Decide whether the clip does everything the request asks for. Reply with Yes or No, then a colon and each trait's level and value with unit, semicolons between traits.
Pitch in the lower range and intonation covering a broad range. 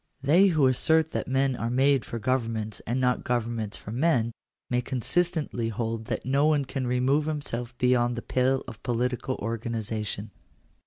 No: low, 125 Hz; average, 2.9 semitones